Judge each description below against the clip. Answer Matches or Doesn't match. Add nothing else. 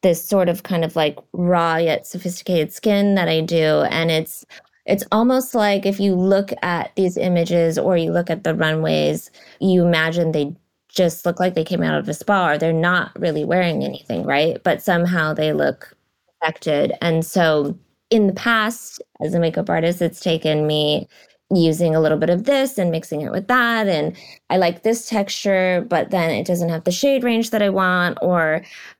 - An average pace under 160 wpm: Doesn't match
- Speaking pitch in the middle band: Matches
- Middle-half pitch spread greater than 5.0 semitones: Doesn't match